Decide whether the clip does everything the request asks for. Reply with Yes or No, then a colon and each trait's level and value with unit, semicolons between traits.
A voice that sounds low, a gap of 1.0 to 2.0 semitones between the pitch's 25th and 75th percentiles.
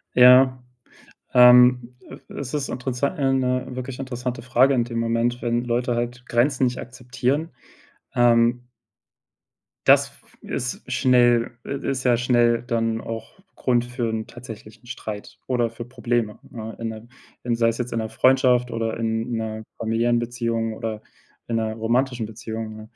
Yes: low, 120 Hz; narrow, 1.6 semitones